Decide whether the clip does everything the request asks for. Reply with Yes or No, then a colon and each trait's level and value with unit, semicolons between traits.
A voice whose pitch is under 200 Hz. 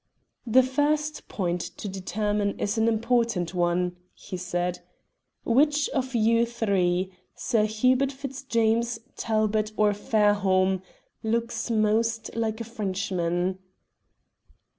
No: high, 215 Hz